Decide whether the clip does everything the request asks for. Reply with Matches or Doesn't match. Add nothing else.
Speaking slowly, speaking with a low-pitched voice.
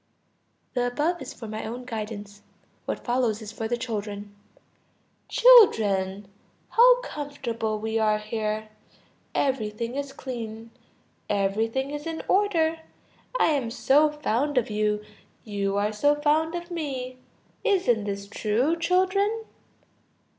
Doesn't match